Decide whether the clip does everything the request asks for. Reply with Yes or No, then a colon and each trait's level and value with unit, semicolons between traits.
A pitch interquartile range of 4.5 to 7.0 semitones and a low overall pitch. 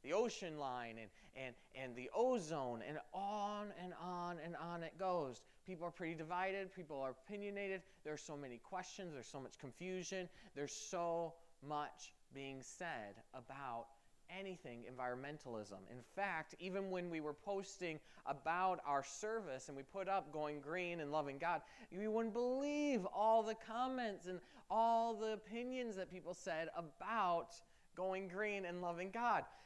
No: average, 5.3 semitones; medium, 175 Hz